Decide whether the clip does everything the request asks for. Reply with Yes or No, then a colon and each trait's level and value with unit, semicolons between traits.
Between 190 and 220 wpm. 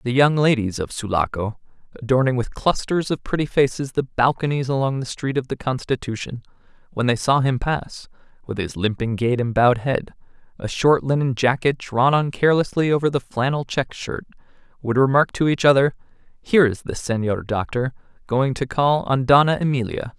No: average, 175 wpm